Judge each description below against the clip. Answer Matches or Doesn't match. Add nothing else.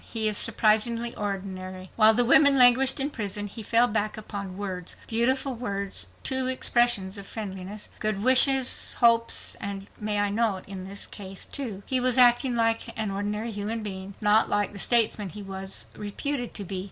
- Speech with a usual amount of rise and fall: Matches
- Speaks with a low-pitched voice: Doesn't match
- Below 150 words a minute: Doesn't match